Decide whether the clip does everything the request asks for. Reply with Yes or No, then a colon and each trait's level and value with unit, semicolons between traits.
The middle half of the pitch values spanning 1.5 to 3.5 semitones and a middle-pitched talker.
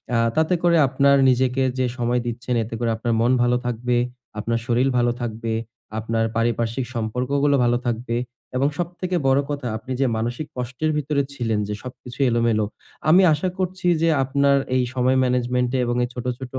No: average, 2.9 semitones; low, 125 Hz